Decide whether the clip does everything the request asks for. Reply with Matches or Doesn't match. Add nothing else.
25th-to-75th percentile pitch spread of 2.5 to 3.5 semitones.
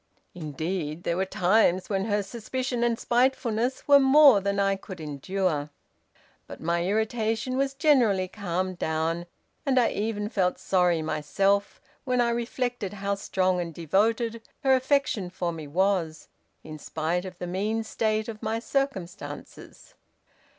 Doesn't match